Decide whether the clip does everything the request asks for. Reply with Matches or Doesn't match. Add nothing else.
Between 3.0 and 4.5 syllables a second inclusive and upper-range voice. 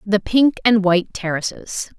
Matches